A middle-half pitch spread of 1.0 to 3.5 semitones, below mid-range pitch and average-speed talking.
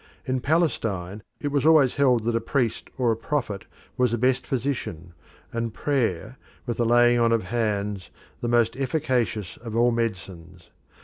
Yes: average, 3.1 semitones; low, 120 Hz; average, 165 wpm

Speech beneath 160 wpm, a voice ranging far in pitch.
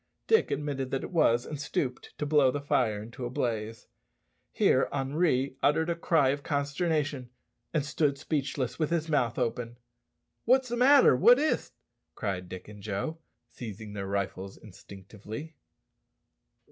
Yes: average, 145 wpm; wide, 5.8 semitones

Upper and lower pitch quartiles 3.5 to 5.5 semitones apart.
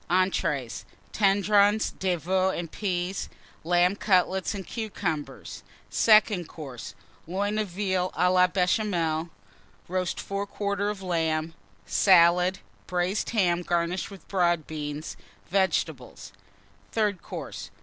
No: narrow, 2.6 semitones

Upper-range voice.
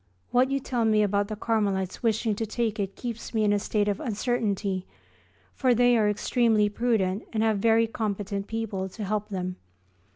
Yes: high, 215 Hz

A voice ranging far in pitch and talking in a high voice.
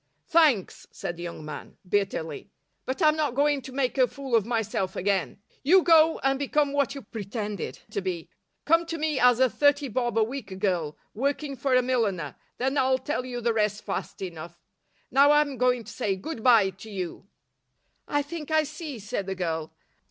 Yes: wide, 6.4 semitones; high, 245 Hz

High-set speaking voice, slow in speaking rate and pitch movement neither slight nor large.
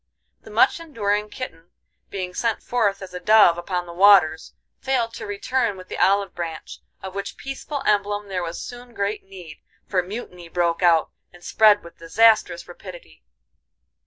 No: high, 195 Hz; average, 160 wpm; average, 3.6 semitones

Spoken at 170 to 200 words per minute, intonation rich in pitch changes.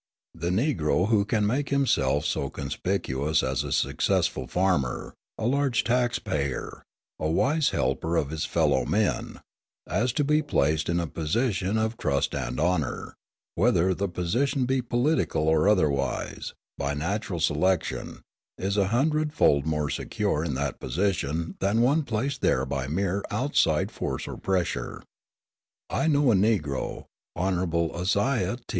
No: average, 145 wpm; wide, 7.5 semitones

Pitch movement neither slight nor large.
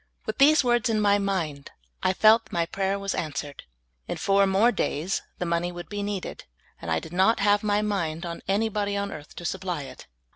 Yes: average, 3.4 semitones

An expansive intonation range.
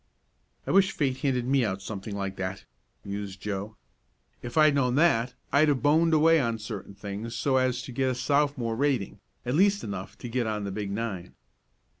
Yes: wide, 5.7 semitones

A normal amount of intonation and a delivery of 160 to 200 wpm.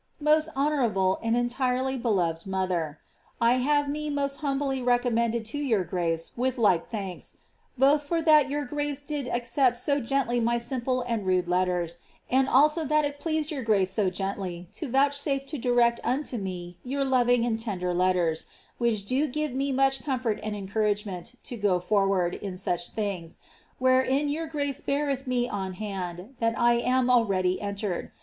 No: wide, 5.9 semitones; average, 165 wpm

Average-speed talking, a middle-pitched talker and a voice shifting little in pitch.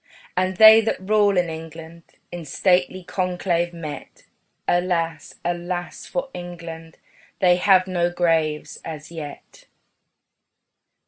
No: slow, 110 wpm; medium, 175 Hz; narrow, 2.0 semitones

